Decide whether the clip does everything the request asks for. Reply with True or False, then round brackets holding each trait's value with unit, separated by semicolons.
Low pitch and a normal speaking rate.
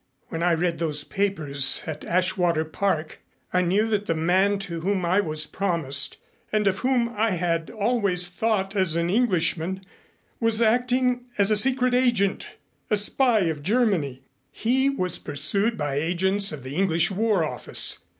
False (190 Hz; 160 wpm)